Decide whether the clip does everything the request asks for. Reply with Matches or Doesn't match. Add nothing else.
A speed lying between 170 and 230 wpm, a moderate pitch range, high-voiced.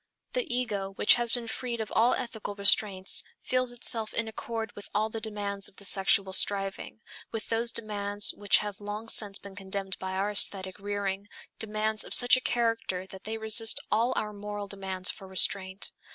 Doesn't match